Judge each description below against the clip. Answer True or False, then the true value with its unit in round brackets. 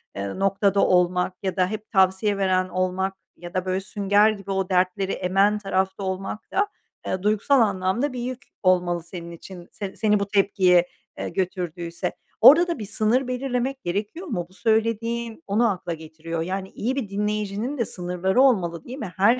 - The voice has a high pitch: True (195 Hz)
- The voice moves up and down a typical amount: True (3.1 semitones)